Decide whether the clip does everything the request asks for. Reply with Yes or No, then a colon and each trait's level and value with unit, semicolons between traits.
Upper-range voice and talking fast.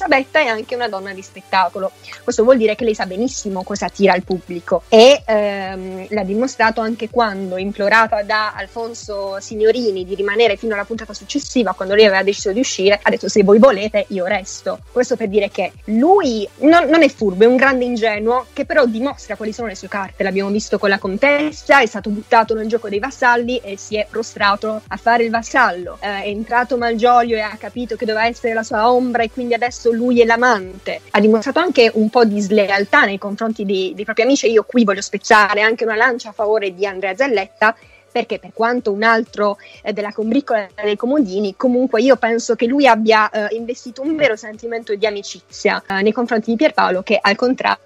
Yes: high, 220 Hz; fast, 205 wpm